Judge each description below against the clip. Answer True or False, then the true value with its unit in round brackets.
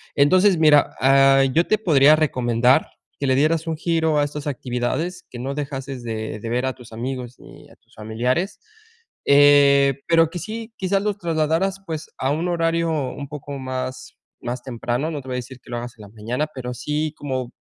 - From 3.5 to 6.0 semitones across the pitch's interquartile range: True (4.1 semitones)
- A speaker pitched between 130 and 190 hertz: True (140 Hz)